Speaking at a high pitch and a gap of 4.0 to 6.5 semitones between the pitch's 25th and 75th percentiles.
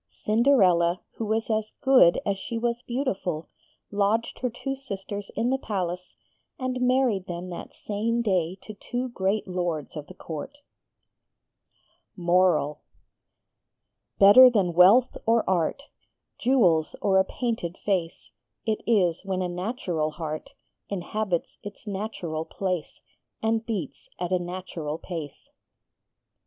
Yes: high, 195 Hz; average, 4.7 semitones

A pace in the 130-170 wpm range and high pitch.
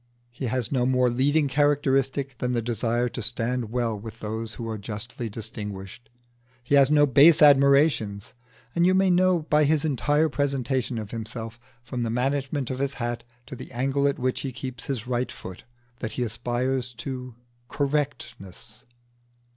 No: average, 165 wpm; low, 125 Hz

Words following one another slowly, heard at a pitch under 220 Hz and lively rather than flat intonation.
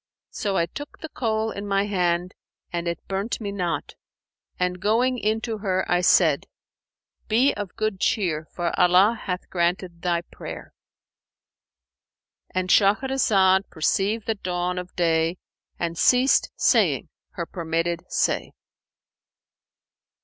No: slow, 125 wpm; high, 190 Hz; average, 3.7 semitones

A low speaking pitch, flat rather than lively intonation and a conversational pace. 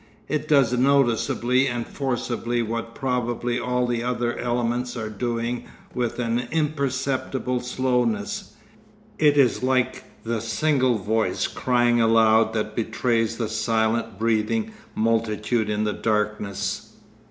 No: low, 120 Hz; narrow, 2.0 semitones; slow, 120 wpm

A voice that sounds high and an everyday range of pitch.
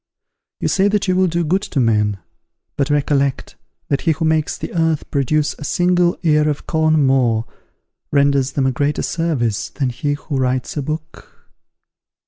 No: medium, 145 Hz; average, 3.3 semitones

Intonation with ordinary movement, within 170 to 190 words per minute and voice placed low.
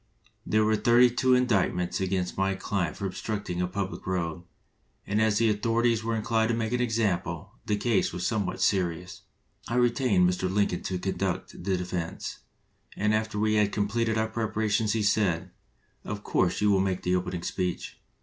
Yes: average, 3.3 semitones; average, 180 wpm; low, 100 Hz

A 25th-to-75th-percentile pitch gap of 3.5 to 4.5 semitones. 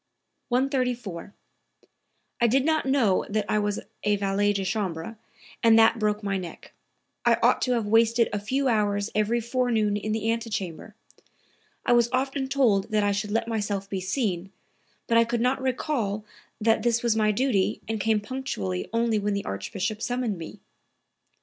No: average, 2.8 semitones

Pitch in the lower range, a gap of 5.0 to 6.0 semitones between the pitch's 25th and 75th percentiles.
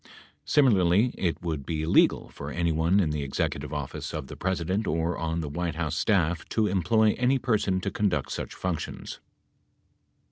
No: very low, 85 Hz; average, 3.9 semitones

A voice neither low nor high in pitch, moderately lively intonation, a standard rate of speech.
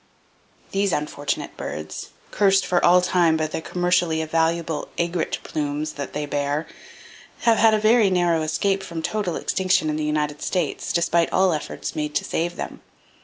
Yes: medium, 170 Hz; average, 3.2 semitones; average, 170 wpm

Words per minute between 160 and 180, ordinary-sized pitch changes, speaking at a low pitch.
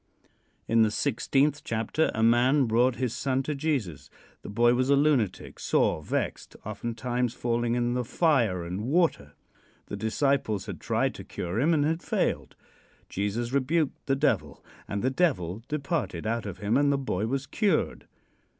Yes: average, 165 wpm; average, 4.3 semitones; low, 120 Hz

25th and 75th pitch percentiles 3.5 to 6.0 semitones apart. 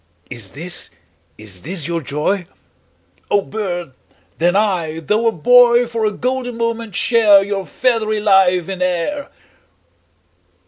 Yes: average, 5.1 semitones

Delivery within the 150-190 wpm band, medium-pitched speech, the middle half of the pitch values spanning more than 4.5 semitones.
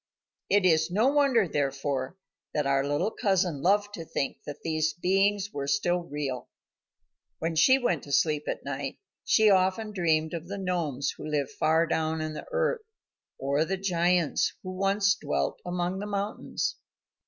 Yes: average, 165 wpm; medium, 170 Hz; average, 5.0 semitones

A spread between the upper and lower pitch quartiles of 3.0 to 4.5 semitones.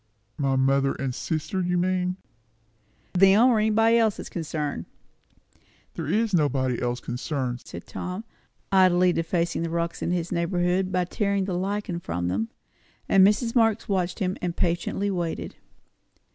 Yes: average, 4.2 semitones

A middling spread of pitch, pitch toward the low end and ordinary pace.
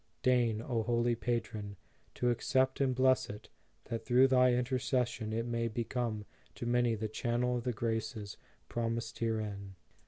No: narrow, 1.8 semitones; low, 120 Hz; average, 155 wpm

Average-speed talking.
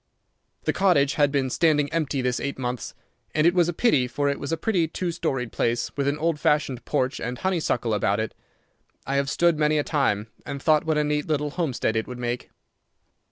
No: fast, 210 wpm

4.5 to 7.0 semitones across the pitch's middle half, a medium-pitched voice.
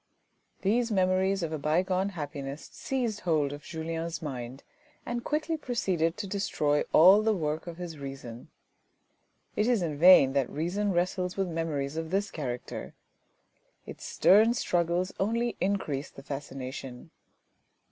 Yes: average, 5.1 semitones; medium, 170 Hz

